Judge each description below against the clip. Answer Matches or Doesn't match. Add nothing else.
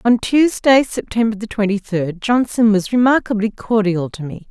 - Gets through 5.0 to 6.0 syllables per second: Doesn't match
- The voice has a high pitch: Matches